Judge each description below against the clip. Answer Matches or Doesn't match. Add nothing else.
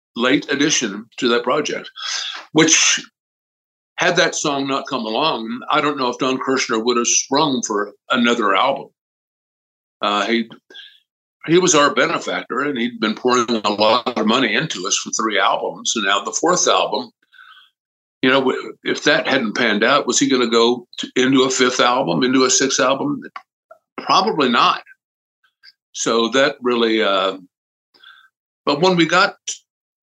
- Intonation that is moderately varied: Matches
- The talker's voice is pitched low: Matches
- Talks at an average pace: Matches